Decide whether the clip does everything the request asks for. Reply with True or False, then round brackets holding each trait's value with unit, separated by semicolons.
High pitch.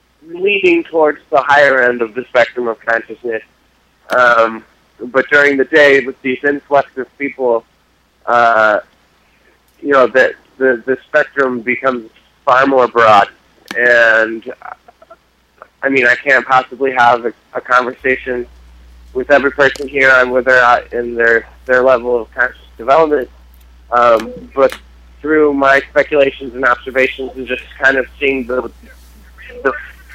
False (130 Hz)